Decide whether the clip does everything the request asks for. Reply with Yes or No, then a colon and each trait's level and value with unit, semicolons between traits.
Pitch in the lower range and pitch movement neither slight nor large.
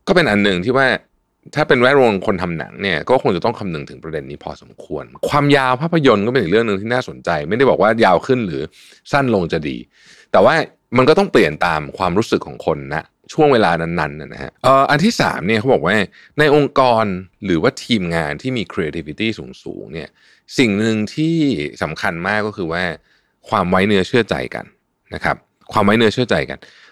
No: low, 110 Hz; wide, 6.8 semitones